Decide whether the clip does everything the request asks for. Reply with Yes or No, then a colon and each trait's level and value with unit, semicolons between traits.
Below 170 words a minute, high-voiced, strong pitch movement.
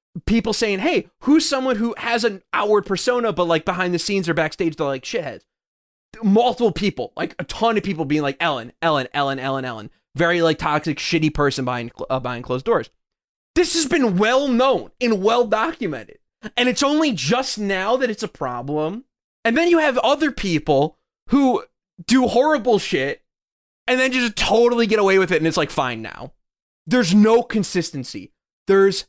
No: average, 180 wpm; high, 205 Hz; wide, 7.4 semitones